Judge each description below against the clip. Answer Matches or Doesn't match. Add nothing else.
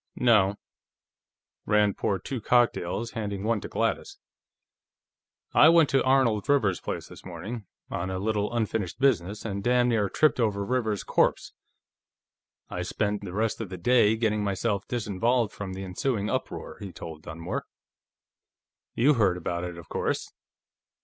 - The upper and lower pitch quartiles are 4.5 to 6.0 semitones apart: Doesn't match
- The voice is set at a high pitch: Doesn't match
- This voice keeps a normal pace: Matches